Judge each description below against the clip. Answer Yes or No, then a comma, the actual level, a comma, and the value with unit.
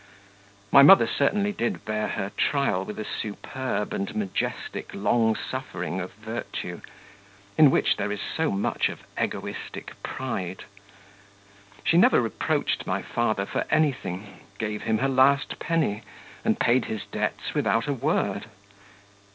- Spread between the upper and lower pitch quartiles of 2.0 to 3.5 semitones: No, average, 5.0 semitones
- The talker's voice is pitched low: Yes, low, 110 Hz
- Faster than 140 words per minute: No, slow, 135 wpm